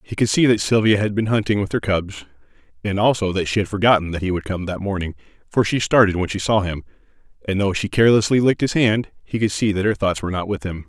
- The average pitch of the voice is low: Yes, low, 100 Hz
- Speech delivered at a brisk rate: Yes, fast, 260 wpm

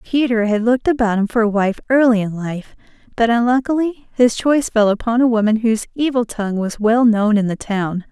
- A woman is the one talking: Yes, female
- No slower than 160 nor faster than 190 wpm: No, fast, 205 wpm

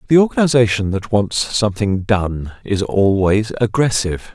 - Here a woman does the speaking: No, male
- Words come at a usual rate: No, slow, 125 wpm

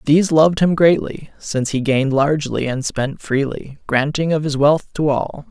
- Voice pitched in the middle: Yes, medium, 145 Hz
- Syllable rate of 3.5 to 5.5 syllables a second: Yes, 5.1 syllables/s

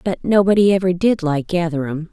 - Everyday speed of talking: Yes, average, 170 wpm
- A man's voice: No, female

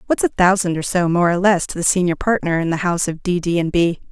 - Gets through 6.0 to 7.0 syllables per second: Yes, 6.3 syllables/s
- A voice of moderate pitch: Yes, medium, 180 Hz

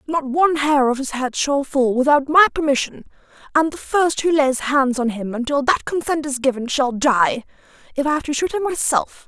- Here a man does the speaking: No, female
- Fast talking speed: Yes, fast, 215 wpm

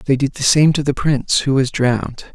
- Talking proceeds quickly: Yes, fast, 255 wpm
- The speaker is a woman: No, male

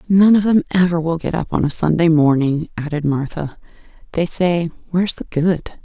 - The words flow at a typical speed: Yes, average, 185 wpm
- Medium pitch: Yes, medium, 165 Hz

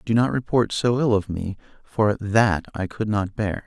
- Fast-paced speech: Yes, fast, 215 wpm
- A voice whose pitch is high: No, low, 105 Hz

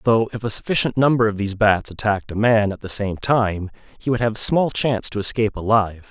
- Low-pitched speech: Yes, low, 110 Hz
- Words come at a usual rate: No, fast, 225 wpm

